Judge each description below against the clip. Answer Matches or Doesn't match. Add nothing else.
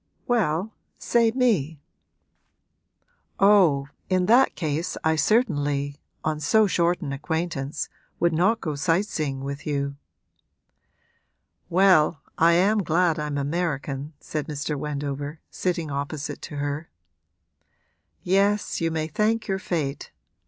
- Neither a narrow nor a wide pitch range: Matches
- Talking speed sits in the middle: Doesn't match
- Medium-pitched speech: Matches